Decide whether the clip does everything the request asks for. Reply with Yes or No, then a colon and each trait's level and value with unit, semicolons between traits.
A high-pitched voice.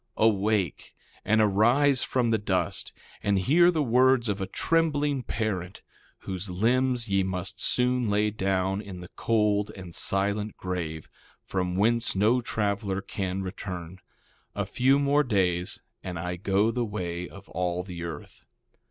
No: low, 100 Hz